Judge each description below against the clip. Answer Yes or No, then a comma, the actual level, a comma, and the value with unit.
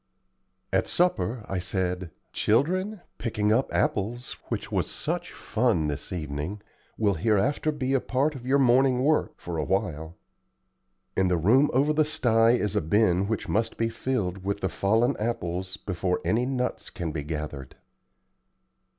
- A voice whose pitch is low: Yes, low, 105 Hz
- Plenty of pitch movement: Yes, wide, 5.9 semitones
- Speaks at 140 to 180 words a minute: Yes, average, 150 wpm